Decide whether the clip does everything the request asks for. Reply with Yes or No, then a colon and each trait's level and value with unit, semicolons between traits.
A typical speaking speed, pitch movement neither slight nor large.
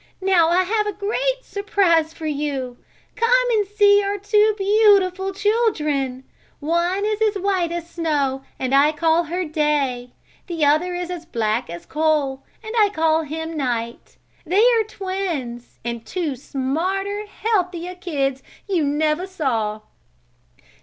No: average, 145 wpm; wide, 5.8 semitones